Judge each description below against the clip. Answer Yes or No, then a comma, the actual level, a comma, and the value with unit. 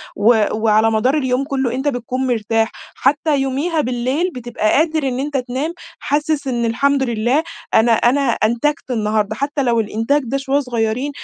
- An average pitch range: Yes, average, 3.6 semitones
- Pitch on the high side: Yes, very high, 255 Hz